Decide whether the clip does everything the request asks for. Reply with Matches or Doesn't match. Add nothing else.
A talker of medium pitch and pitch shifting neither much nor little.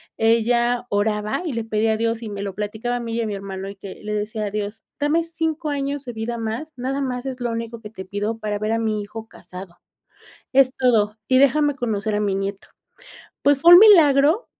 Doesn't match